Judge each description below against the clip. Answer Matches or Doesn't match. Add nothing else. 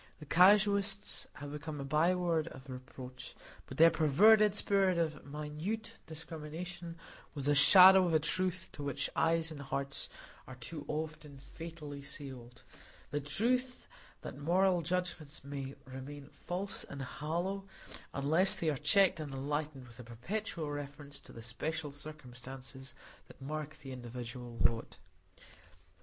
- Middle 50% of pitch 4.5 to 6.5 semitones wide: Doesn't match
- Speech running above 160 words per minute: Doesn't match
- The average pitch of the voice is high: Doesn't match